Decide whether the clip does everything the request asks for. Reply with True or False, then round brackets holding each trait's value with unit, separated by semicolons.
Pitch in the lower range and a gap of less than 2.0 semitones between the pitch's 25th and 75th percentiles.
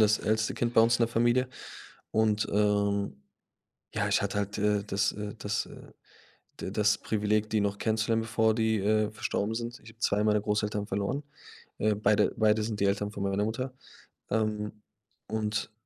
True (105 Hz; 1.3 semitones)